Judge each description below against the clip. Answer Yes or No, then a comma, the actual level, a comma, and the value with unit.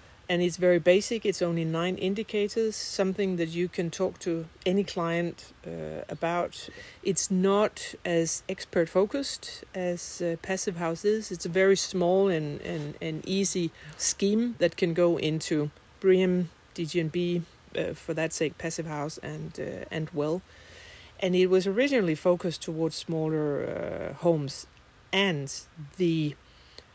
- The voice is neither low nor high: Yes, medium, 175 Hz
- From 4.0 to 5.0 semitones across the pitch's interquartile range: No, average, 2.8 semitones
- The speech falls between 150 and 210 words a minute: No, average, 140 wpm